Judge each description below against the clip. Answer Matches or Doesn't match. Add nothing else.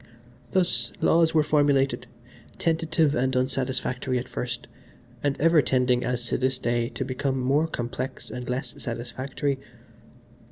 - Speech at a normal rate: Doesn't match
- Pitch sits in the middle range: Doesn't match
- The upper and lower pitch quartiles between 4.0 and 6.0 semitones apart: Doesn't match